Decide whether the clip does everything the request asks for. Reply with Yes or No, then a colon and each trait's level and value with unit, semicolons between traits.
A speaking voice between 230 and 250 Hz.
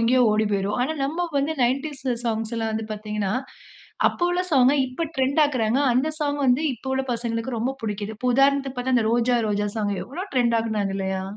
Yes: high, 240 Hz